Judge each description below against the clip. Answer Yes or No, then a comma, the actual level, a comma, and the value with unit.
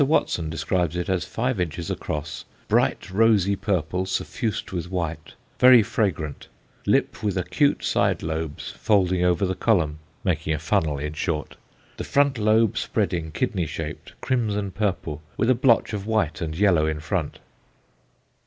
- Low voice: Yes, very low, 90 Hz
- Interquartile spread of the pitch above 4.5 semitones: Yes, average, 5.1 semitones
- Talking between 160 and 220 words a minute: No, average, 150 wpm